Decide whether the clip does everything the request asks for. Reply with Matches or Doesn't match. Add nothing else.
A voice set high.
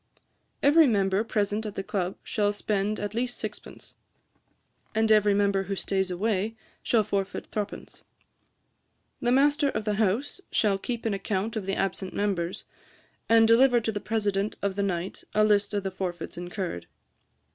Matches